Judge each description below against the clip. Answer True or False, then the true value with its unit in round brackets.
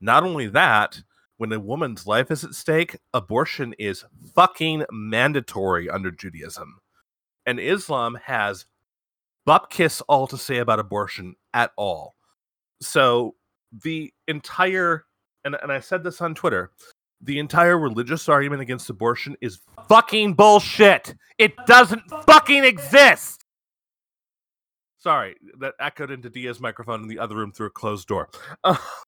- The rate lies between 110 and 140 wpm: True (135 wpm)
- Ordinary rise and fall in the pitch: False (7.6 semitones)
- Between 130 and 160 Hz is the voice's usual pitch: True (140 Hz)